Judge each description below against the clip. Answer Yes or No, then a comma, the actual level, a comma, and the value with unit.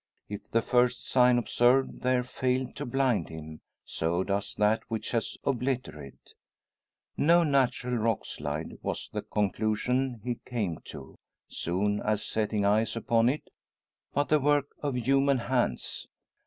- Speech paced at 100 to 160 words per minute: Yes, average, 140 wpm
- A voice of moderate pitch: No, low, 120 Hz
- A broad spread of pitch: No, average, 3.8 semitones